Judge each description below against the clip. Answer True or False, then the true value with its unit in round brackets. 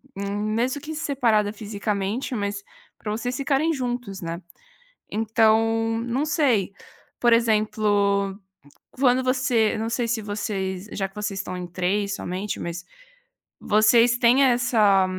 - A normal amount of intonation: True (3.3 semitones)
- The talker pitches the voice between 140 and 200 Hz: False (215 Hz)